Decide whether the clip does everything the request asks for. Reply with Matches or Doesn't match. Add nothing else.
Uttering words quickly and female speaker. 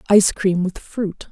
Doesn't match